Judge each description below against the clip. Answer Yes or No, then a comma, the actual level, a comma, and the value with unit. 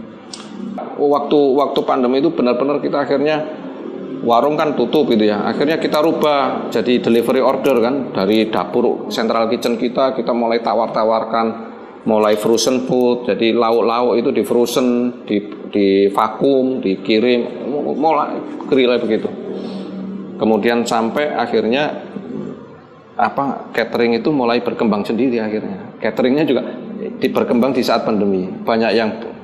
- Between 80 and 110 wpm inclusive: No, average, 125 wpm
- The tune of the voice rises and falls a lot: No, average, 2.9 semitones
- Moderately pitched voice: No, low, 120 Hz